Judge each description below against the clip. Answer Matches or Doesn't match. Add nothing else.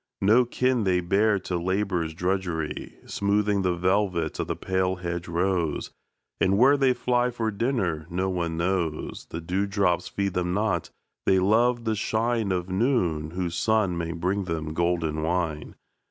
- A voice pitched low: Matches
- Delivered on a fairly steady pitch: Doesn't match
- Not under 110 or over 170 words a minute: Matches